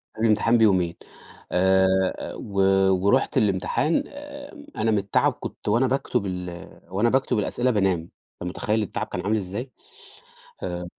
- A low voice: Yes, low, 105 Hz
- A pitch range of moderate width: Yes, average, 4.4 semitones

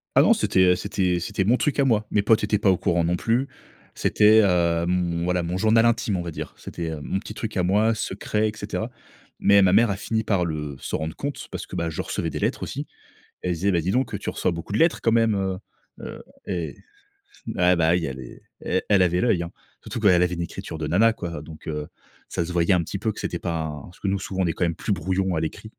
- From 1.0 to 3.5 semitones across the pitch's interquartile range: No, average, 3.9 semitones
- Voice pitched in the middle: No, very low, 90 Hz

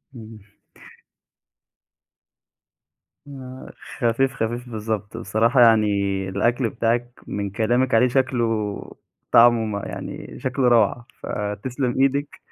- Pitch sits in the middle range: No, low, 120 Hz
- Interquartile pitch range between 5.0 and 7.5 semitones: No, narrow, 2.5 semitones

